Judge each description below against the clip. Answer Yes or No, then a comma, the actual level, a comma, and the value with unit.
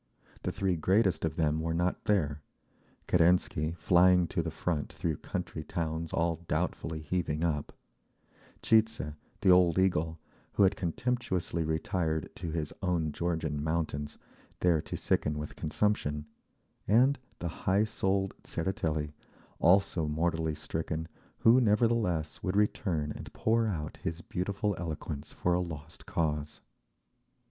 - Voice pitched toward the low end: Yes, very low, 85 Hz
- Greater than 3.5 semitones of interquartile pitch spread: No, average, 3.2 semitones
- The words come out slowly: Yes, slow, 130 wpm